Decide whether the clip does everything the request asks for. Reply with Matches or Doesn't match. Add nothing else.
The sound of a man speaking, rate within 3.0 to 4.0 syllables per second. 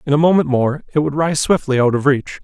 Doesn't match